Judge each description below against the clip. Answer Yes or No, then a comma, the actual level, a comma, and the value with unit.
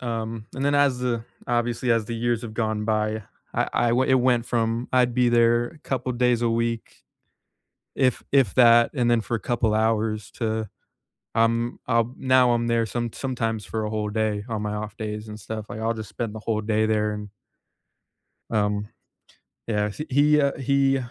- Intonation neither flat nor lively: No, narrow, 2.0 semitones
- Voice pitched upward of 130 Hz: No, low, 115 Hz